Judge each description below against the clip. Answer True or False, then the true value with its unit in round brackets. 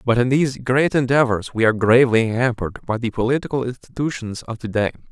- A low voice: True (120 Hz)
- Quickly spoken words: False (175 wpm)